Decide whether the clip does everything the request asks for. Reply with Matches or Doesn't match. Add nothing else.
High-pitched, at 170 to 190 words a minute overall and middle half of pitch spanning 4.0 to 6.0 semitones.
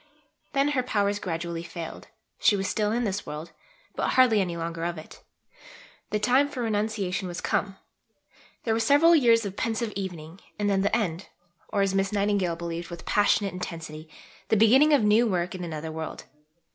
Matches